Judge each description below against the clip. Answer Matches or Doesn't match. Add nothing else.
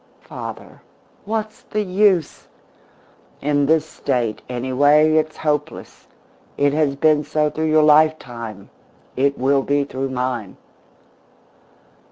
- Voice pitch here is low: Doesn't match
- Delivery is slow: Matches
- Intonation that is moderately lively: Matches